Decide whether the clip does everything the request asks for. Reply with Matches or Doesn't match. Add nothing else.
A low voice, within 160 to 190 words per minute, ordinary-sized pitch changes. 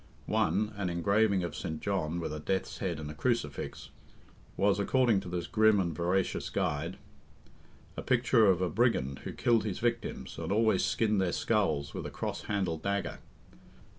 Matches